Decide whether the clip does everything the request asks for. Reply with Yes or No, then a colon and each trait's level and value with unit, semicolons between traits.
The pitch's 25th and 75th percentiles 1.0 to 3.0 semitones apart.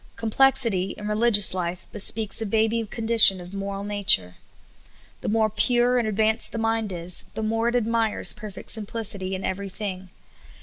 Yes: narrow, 2.5 semitones